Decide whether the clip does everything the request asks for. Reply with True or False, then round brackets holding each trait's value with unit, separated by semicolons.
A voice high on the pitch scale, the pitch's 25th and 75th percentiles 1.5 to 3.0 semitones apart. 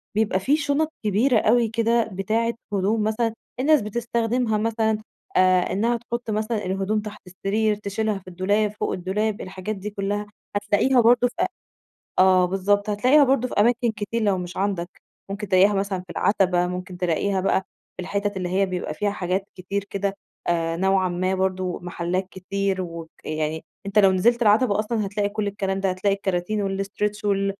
True (200 Hz; 2.6 semitones)